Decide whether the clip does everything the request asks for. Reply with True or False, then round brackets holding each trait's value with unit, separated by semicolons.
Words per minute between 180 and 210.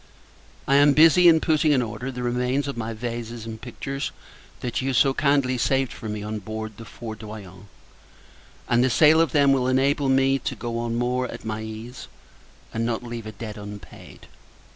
True (185 wpm)